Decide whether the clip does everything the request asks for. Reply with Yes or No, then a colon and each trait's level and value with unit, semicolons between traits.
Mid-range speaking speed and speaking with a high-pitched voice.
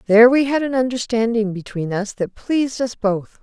Yes: average, 190 wpm; high, 230 Hz